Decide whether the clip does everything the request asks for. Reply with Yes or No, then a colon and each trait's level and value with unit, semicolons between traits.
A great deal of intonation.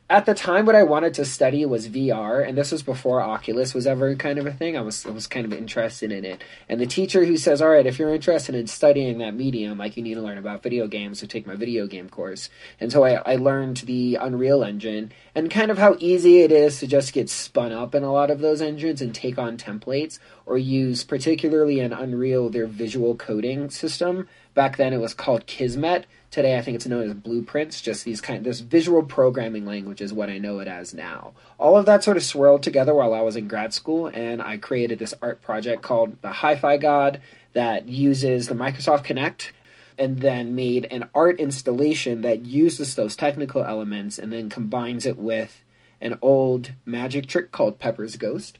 No: average, 4.2 semitones